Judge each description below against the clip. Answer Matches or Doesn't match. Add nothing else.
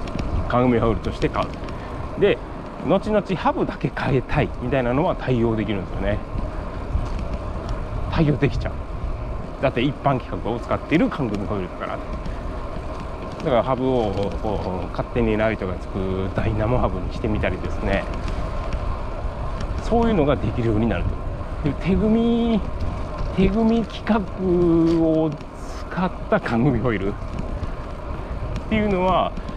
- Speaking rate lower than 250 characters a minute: Doesn't match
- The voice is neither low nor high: Doesn't match